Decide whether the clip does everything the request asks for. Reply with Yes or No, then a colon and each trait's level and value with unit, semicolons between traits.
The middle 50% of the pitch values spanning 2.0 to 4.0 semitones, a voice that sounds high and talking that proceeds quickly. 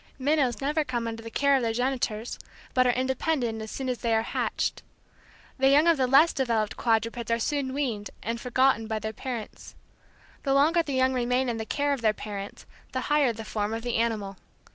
Yes: average, 3.2 semitones; high, 245 Hz; fast, 210 wpm